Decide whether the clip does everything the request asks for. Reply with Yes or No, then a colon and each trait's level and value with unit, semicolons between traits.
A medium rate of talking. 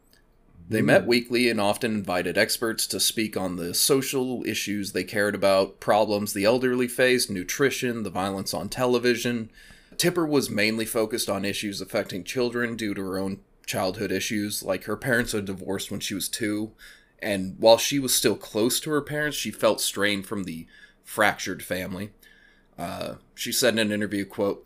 Yes: average, 175 wpm